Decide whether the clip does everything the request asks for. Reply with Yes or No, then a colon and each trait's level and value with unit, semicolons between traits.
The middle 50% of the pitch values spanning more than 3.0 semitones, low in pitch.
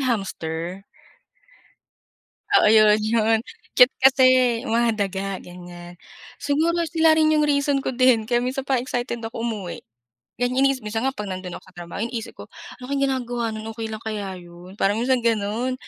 No: average, 4.5 semitones; high, 230 Hz